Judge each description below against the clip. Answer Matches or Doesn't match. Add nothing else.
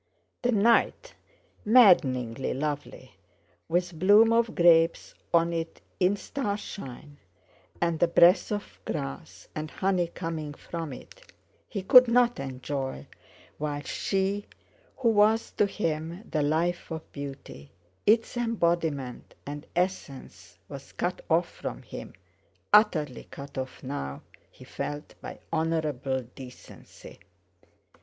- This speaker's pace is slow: Matches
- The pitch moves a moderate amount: Doesn't match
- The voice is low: Doesn't match